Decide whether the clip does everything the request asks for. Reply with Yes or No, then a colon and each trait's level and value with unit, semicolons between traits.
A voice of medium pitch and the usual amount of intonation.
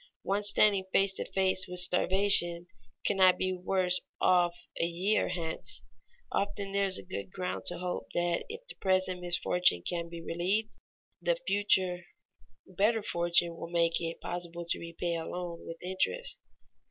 No: medium, 180 Hz; narrow, 2.1 semitones